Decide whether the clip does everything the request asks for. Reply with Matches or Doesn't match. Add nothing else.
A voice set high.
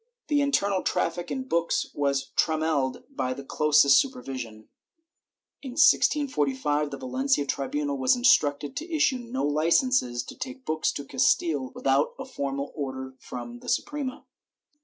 Doesn't match